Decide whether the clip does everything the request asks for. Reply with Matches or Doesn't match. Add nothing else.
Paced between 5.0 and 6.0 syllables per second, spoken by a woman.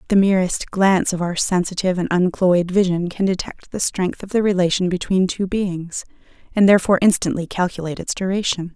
Matches